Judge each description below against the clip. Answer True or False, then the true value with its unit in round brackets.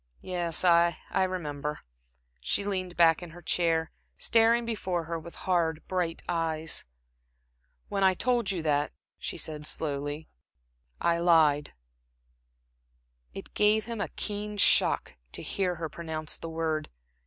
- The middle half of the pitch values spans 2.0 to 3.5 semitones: True (2.9 semitones)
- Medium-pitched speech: True (170 Hz)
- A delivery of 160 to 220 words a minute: False (140 wpm)